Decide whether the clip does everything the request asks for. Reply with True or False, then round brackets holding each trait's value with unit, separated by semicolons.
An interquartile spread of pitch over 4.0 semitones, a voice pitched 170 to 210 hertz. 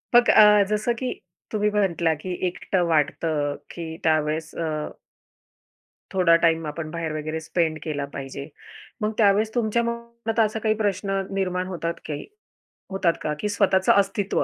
True (4.7 semitones; 185 Hz)